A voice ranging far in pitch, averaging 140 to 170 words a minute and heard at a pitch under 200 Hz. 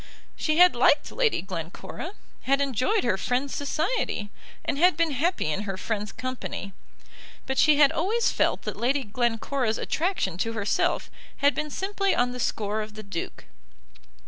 No: wide, 6.8 semitones; average, 155 wpm; very high, 255 Hz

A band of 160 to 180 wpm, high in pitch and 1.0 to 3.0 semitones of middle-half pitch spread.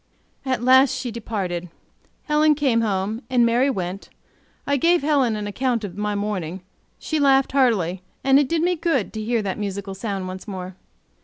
No: average, 175 wpm; high, 230 Hz; wide, 5.5 semitones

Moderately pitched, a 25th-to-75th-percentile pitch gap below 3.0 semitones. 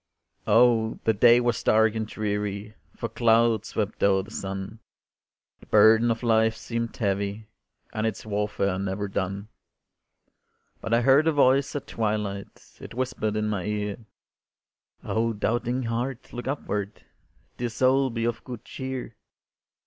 No: low, 110 Hz; narrow, 2.6 semitones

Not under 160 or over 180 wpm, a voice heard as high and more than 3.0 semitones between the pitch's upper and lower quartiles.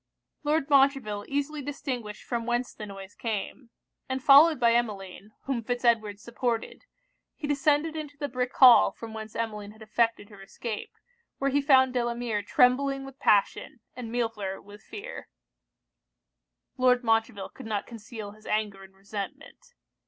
No: average, 150 wpm; high, 235 Hz; average, 4.3 semitones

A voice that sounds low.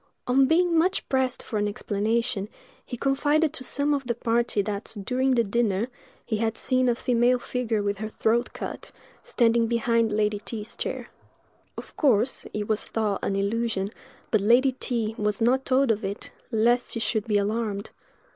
No: high, 230 Hz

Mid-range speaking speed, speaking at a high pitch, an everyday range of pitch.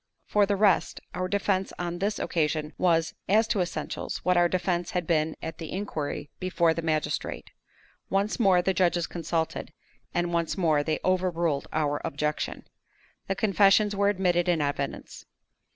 No: average, 155 wpm; medium, 175 Hz; average, 3.1 semitones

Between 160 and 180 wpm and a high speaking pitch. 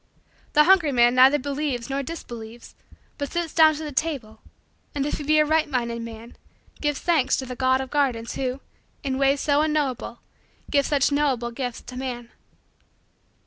Yes: average, 175 wpm; very high, 275 Hz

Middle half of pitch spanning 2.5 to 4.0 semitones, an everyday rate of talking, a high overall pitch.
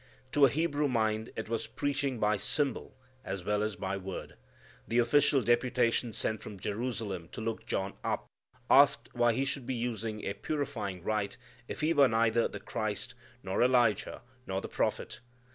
No: average, 3.6 semitones; average, 170 wpm; low, 115 Hz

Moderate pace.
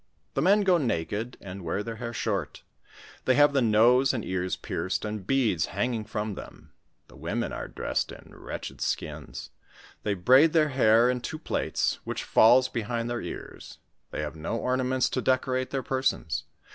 Yes: average, 170 wpm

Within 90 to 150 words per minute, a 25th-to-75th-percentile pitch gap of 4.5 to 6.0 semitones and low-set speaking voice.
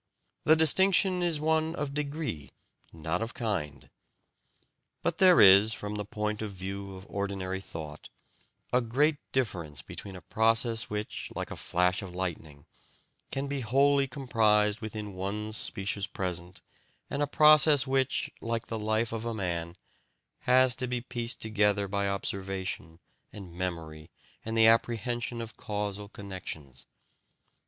Yes: average, 140 wpm; average, 4.9 semitones; low, 105 Hz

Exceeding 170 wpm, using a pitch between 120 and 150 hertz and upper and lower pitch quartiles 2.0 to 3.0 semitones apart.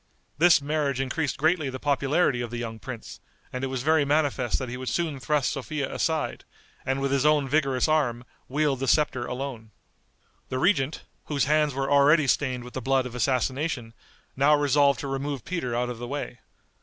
Yes: average, 190 wpm; low, 135 Hz; average, 2.7 semitones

